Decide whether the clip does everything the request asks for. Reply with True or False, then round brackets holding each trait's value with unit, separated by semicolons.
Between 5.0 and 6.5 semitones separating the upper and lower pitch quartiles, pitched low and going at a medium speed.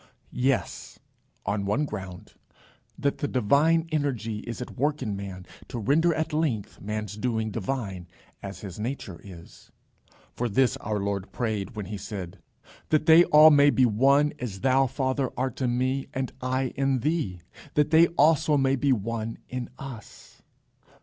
True (5.3 semitones; 125 Hz; 160 wpm)